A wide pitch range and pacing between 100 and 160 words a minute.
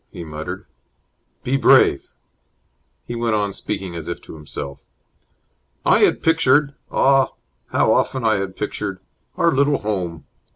Yes: wide, 7.8 semitones; slow, 135 wpm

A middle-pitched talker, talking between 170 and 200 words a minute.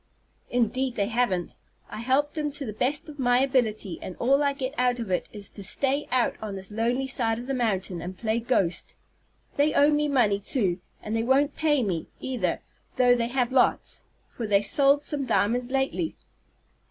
No: high, 245 Hz; average, 190 wpm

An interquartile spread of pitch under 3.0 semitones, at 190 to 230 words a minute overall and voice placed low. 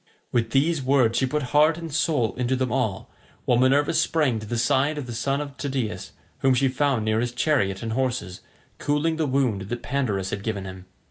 No: average, 4.1 semitones; fast, 205 wpm; low, 130 Hz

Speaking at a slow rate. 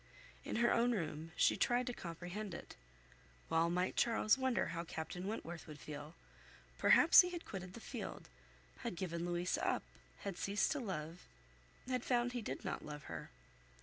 No: average, 170 wpm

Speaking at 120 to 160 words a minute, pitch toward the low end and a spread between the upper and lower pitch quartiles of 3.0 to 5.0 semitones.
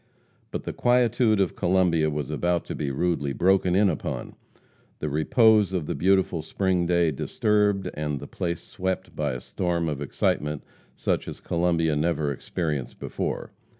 Yes: average, 155 wpm; very low, 85 Hz; average, 3.8 semitones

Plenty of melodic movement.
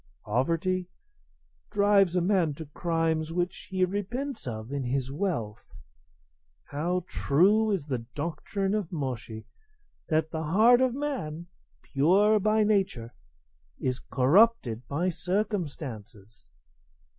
Yes: wide, 6.6 semitones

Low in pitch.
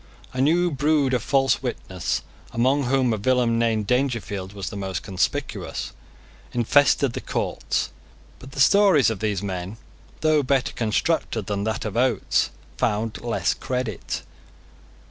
Yes: low, 120 Hz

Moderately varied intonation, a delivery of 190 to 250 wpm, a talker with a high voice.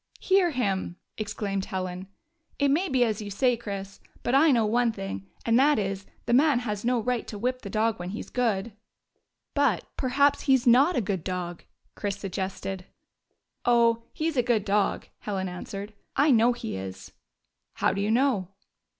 Yes: average, 4.4 semitones; average, 200 wpm; high, 225 Hz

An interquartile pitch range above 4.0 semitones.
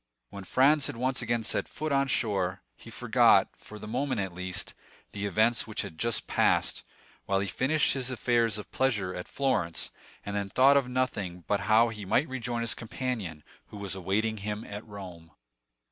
Yes: average, 4.5 semitones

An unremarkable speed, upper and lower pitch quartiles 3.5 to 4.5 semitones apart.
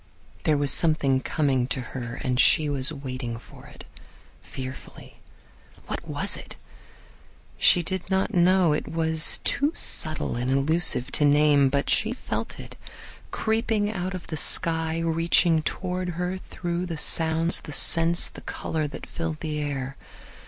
Yes: average, 150 wpm; average, 3.8 semitones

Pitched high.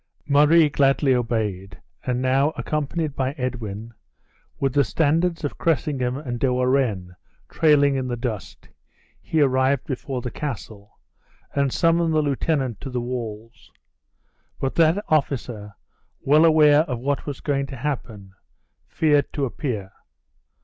No: low, 135 Hz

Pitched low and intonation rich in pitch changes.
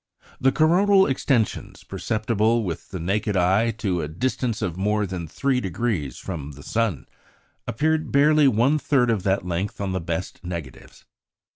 Yes: low, 105 Hz; wide, 6.2 semitones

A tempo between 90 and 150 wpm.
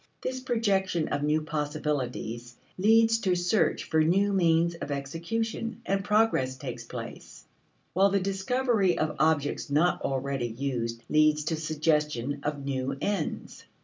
Yes: slow, 135 wpm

